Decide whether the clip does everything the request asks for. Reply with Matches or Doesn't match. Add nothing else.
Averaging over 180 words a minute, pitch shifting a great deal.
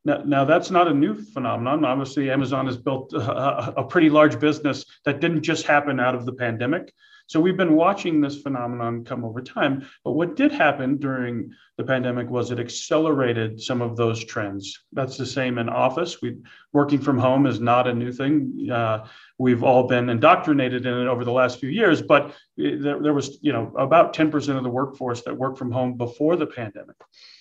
Doesn't match